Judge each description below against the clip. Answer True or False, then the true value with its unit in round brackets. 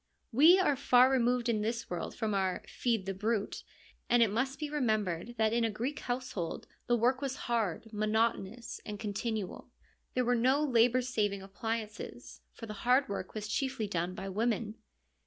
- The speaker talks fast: False (180 wpm)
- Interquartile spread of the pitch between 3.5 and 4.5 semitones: False (3.0 semitones)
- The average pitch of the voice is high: True (230 Hz)